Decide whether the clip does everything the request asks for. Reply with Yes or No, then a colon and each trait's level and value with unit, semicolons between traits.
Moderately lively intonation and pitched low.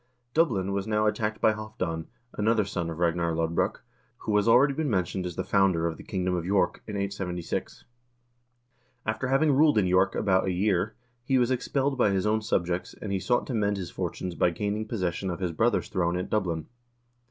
Yes: average, 3.4 semitones; low, 100 Hz